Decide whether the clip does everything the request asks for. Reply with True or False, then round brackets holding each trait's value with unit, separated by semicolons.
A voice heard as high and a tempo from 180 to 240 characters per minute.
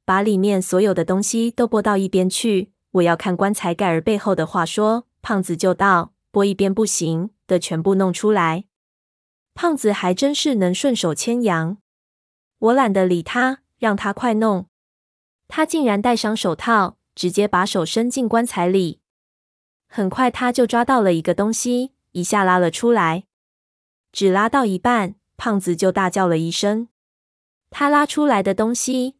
True (200 Hz; 235 characters per minute)